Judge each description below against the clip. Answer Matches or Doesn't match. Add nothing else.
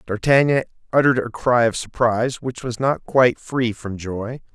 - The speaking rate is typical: Matches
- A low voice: Matches